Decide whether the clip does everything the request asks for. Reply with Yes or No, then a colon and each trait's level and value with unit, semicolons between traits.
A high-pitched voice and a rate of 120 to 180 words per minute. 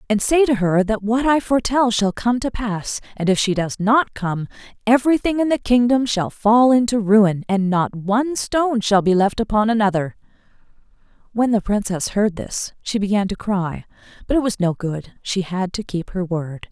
No: high, 215 Hz; average, 195 wpm